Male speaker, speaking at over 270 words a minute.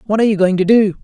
Yes: male; fast, 350 wpm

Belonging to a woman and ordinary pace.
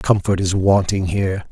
No: male; average, 160 wpm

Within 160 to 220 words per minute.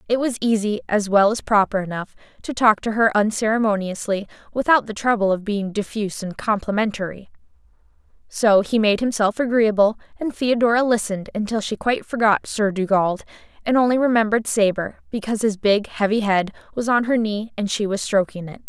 Yes: average, 170 wpm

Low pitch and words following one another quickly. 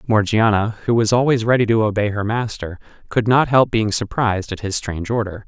No: low, 110 Hz; average, 195 wpm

